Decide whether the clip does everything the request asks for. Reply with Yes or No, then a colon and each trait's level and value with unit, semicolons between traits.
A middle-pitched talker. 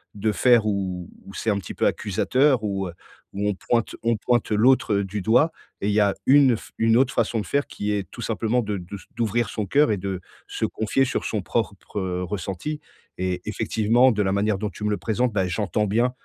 No: low, 105 Hz